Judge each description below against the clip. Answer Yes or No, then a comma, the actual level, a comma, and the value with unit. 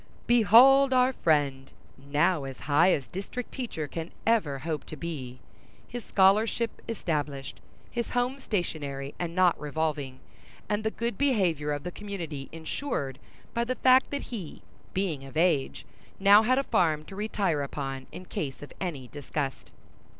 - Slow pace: No, average, 150 wpm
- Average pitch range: No, wide, 7.3 semitones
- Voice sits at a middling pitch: Yes, medium, 170 Hz